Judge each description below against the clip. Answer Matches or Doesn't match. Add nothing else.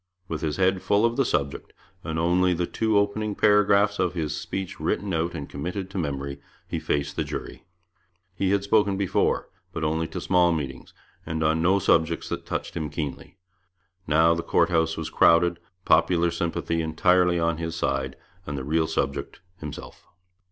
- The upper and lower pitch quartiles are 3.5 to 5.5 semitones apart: Doesn't match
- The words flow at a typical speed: Matches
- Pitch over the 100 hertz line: Doesn't match